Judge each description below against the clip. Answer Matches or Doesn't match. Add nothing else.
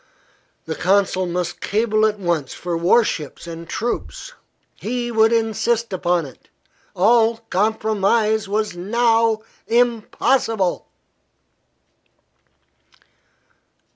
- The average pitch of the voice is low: Doesn't match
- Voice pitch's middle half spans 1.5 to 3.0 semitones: Doesn't match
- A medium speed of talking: Doesn't match